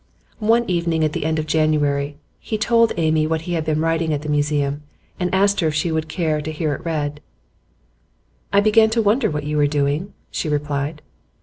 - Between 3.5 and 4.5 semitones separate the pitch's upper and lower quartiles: No, average, 2.8 semitones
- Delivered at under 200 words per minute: No, fast, 205 wpm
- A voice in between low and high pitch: Yes, medium, 155 Hz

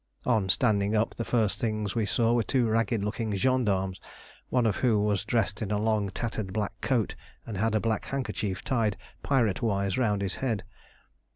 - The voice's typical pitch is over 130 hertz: No, low, 110 Hz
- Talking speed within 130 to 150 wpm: No, average, 185 wpm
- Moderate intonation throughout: No, narrow, 2.3 semitones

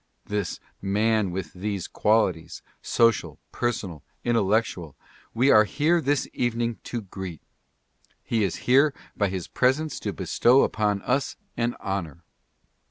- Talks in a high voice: No, low, 110 Hz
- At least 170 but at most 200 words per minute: No, slow, 135 wpm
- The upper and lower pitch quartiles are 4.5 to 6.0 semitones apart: No, average, 3.9 semitones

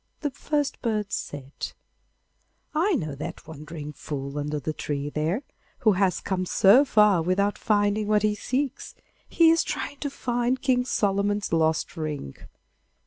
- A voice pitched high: Yes, high, 200 Hz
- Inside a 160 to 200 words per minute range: No, average, 145 wpm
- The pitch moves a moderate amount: No, wide, 7.9 semitones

